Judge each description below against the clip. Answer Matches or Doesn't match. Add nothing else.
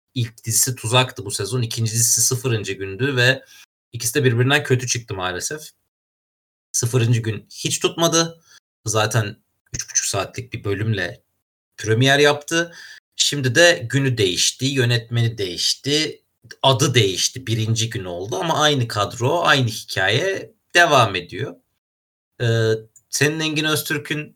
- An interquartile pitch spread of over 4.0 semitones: Matches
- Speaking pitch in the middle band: Doesn't match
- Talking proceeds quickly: Doesn't match